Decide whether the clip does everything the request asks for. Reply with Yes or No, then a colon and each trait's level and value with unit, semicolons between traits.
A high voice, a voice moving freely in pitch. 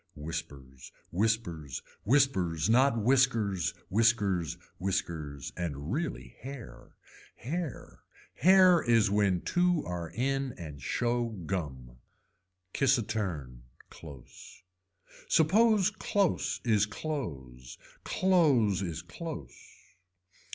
No: low, 105 Hz; wide, 9.0 semitones